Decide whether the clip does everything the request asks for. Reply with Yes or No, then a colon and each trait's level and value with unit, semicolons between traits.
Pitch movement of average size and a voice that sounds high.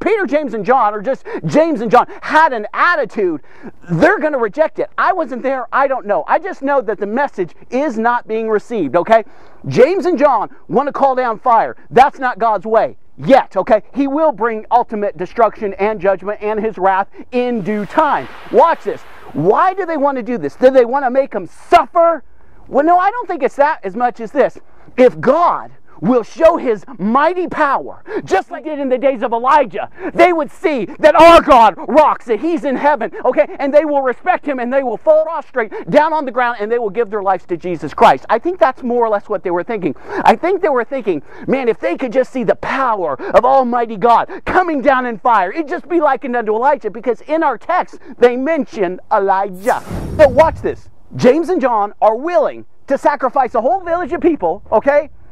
No: wide, 5.8 semitones; very high, 265 Hz